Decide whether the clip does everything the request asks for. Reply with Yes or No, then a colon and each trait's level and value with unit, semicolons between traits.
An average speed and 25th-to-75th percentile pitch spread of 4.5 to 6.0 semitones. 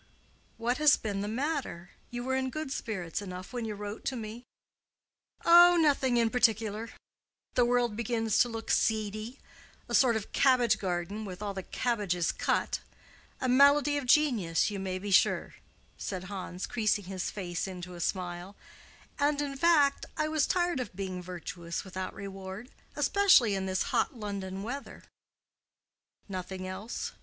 Yes: average, 155 wpm; average, 5.2 semitones